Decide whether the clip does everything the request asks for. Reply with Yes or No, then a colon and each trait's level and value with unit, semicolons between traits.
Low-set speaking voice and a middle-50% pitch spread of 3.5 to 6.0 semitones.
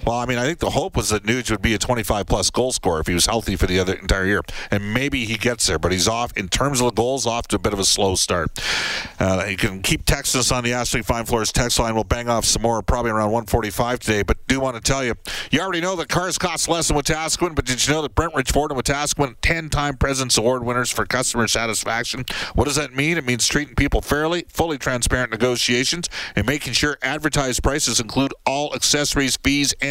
Yes: low, 125 Hz; average, 4.1 semitones